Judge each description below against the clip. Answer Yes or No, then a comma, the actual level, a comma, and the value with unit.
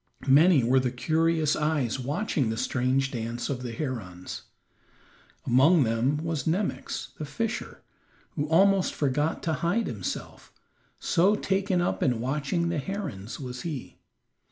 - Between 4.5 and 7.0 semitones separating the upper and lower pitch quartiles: Yes, average, 5.2 semitones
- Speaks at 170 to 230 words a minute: No, slow, 135 wpm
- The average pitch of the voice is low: No, medium, 145 Hz